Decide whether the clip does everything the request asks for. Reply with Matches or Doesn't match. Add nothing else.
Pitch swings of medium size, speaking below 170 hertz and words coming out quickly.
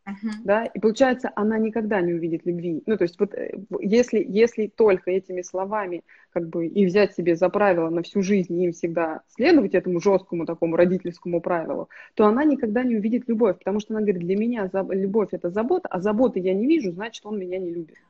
Doesn't match